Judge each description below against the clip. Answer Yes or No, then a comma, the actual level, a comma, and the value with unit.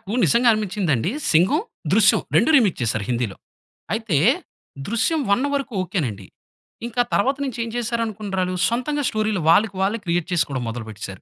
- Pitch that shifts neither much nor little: No, wide, 6.2 semitones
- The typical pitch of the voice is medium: No, high, 200 Hz